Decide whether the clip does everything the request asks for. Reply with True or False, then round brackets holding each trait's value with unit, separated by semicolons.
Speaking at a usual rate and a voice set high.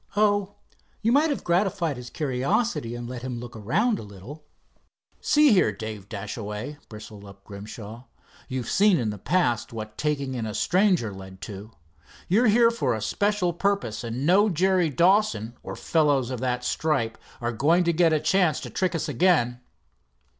False (170 wpm; 140 Hz)